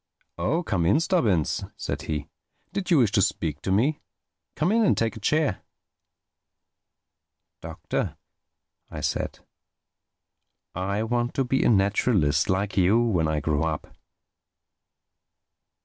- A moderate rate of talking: No, slow, 115 wpm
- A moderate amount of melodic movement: No, wide, 7.7 semitones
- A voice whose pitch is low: Yes, low, 100 Hz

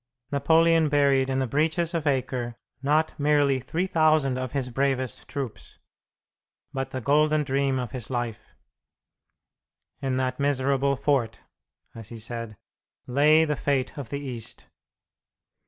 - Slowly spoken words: Yes, slow, 130 wpm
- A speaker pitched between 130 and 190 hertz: Yes, low, 135 Hz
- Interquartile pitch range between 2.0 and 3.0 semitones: Yes, narrow, 2.5 semitones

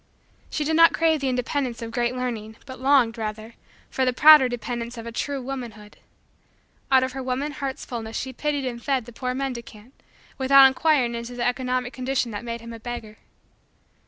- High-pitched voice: Yes, very high, 250 Hz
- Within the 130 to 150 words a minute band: No, average, 190 wpm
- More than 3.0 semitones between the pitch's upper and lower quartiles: No, narrow, 2.5 semitones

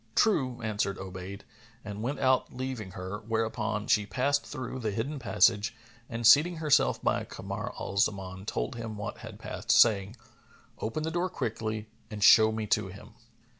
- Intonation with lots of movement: No, average, 4.0 semitones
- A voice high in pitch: No, low, 110 Hz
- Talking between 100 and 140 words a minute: No, average, 165 wpm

